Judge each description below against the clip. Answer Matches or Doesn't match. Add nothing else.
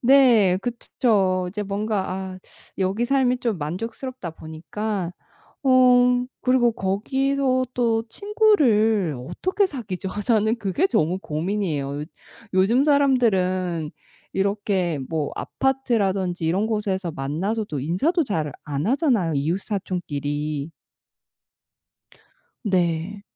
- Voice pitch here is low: Doesn't match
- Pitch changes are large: Matches